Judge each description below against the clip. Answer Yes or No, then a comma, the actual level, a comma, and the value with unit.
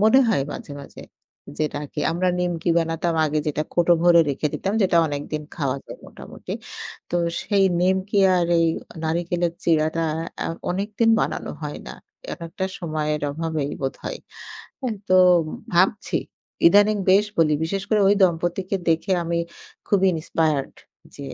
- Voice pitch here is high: No, medium, 170 Hz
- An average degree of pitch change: Yes, average, 3.3 semitones